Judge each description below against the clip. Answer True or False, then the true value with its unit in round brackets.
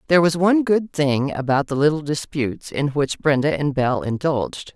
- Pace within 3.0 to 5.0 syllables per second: False (5.5 syllables/s)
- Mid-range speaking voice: True (150 Hz)